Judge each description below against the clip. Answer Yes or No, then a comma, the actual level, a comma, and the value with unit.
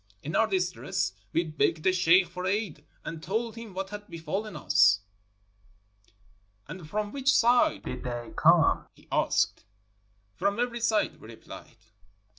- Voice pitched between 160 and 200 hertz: Yes, medium, 185 Hz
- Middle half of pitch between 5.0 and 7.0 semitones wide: Yes, average, 5.3 semitones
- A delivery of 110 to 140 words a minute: No, average, 155 wpm